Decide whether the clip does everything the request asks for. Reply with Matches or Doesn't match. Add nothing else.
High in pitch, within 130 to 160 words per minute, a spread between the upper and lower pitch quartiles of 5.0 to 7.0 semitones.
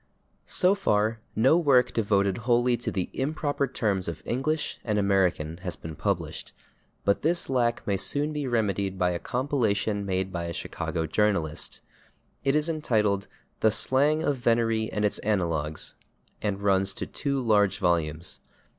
Doesn't match